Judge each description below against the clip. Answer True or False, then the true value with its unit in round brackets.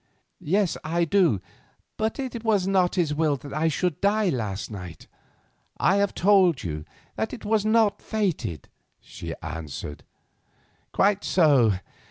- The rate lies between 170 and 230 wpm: False (140 wpm)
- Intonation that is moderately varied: False (8.5 semitones)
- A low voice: False (175 Hz)